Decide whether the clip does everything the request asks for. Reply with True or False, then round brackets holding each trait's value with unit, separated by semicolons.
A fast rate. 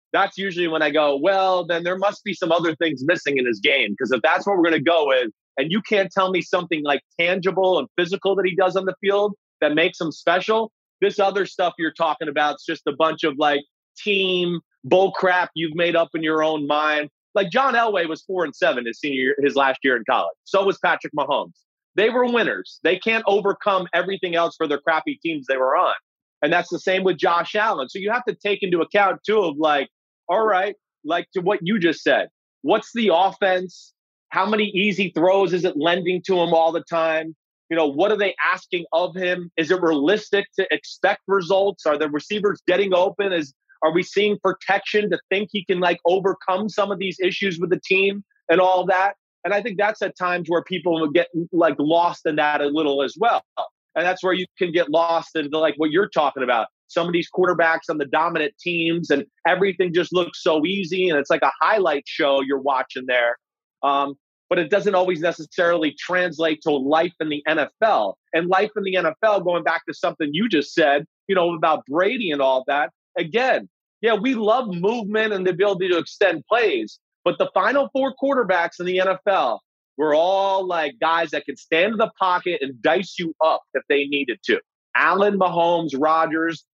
True (215 wpm)